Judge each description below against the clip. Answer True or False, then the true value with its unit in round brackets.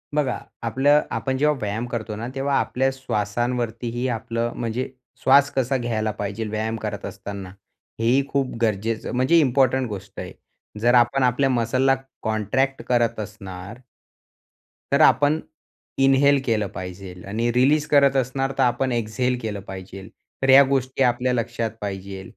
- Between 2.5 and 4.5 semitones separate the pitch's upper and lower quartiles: True (3.6 semitones)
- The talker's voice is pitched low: True (120 Hz)